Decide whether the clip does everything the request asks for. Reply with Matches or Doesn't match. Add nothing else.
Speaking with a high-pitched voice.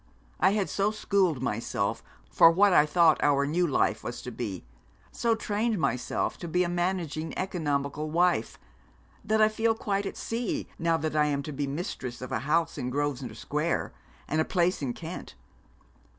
Doesn't match